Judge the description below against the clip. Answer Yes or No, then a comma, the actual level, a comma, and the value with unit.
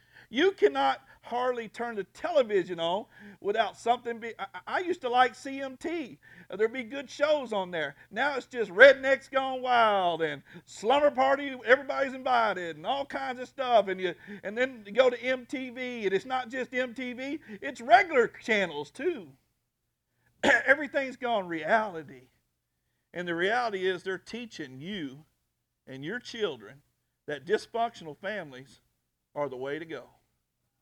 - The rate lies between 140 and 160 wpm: Yes, average, 150 wpm